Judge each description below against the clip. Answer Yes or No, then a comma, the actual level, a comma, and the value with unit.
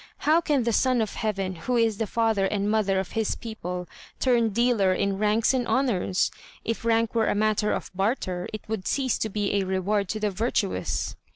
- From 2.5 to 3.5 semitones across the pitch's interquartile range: Yes, average, 2.9 semitones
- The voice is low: No, high, 215 Hz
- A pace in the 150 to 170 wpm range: No, average, 200 wpm